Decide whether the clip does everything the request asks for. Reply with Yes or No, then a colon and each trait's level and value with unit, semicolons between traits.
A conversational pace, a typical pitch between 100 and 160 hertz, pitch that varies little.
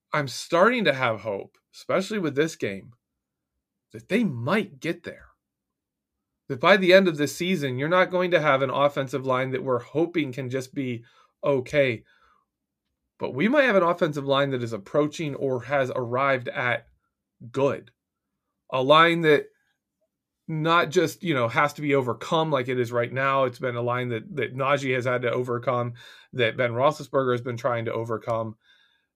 No: average, 175 wpm; medium, 140 Hz; average, 4.4 semitones